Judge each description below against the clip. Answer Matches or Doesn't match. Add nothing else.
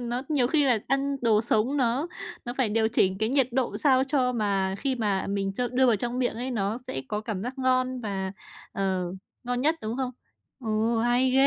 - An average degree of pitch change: Matches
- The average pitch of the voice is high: Matches